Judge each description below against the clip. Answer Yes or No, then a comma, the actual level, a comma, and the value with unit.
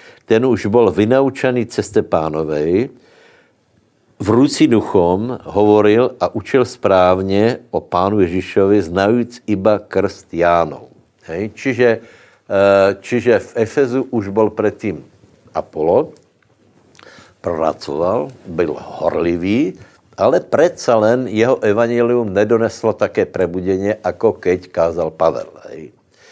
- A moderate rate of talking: No, slow, 100 wpm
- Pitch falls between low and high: No, low, 105 Hz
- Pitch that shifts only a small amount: No, average, 3.7 semitones